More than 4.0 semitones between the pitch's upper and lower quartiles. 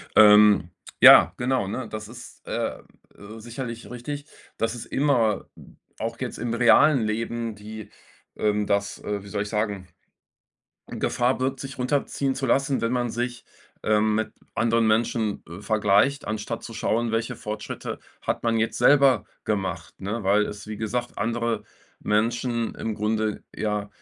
No: narrow, 2.4 semitones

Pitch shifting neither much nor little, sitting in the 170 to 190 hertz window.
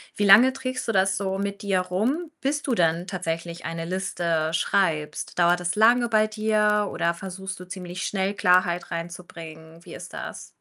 Yes: average, 3.6 semitones; medium, 185 Hz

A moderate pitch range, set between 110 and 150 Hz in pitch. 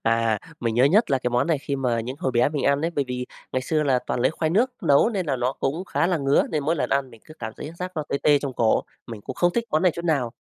Yes: average, 4.4 semitones; medium, 140 Hz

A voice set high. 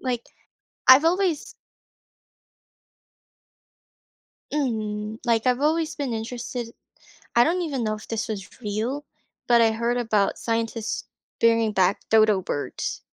Yes: high, 230 Hz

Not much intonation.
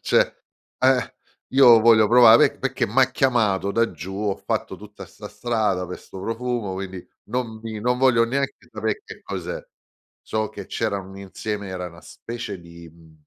No: average, 3.8 semitones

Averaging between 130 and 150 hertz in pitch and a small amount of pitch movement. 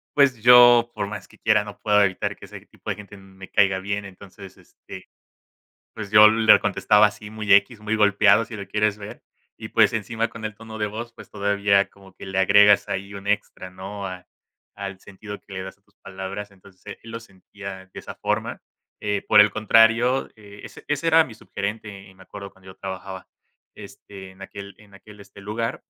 No: low, 100 Hz; narrow, 1.8 semitones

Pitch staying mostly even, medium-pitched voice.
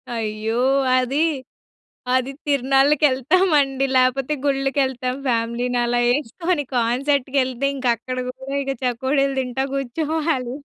No: narrow, 2.0 semitones; very high, 265 Hz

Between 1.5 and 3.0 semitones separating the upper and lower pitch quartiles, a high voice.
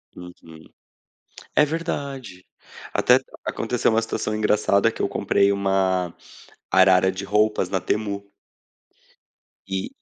No: narrow, 2.5 semitones; low, 100 Hz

